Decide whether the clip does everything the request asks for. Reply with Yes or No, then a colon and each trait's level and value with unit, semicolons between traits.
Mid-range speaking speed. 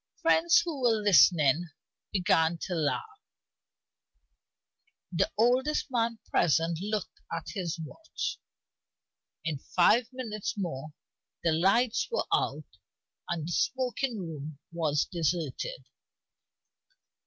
No: slow, 100 wpm